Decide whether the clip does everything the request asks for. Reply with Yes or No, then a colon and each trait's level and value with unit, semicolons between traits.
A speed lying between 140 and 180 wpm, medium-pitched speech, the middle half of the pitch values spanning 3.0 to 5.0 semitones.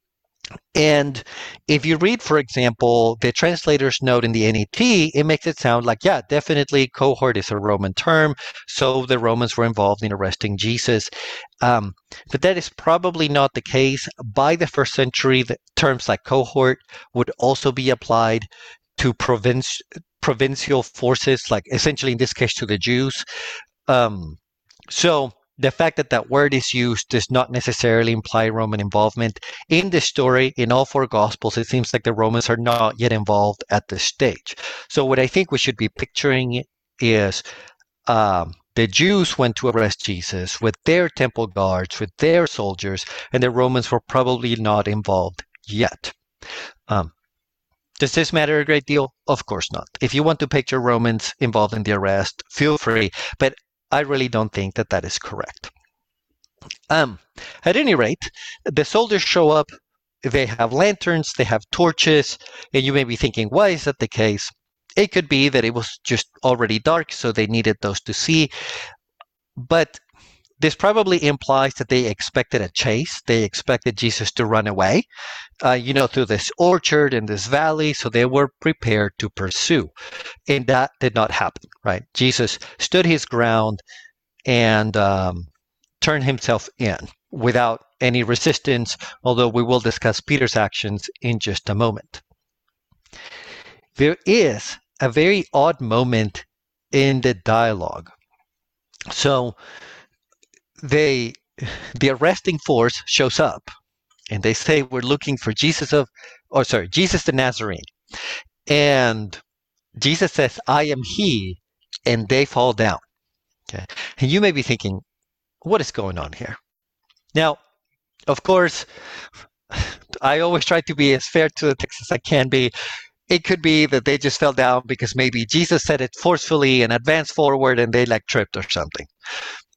No: average, 160 wpm; low, 125 Hz; average, 4.6 semitones